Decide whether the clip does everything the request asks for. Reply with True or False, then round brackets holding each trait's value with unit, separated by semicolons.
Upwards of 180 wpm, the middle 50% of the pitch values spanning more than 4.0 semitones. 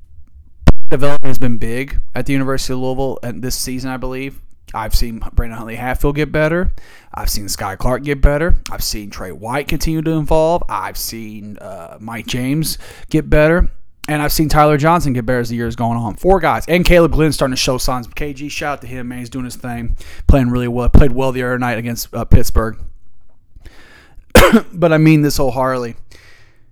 True (200 wpm; 4.6 semitones)